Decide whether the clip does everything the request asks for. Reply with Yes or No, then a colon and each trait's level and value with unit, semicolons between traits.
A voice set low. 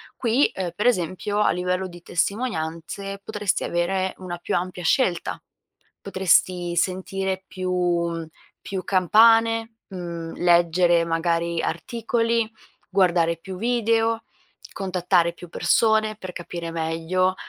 No: medium, 185 Hz